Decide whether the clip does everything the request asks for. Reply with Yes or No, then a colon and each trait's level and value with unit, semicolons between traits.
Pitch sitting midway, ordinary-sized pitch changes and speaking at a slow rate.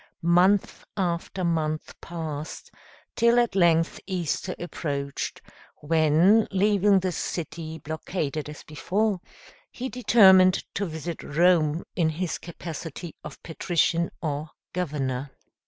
Yes: medium, 170 Hz; average, 3.2 semitones; slow, 105 wpm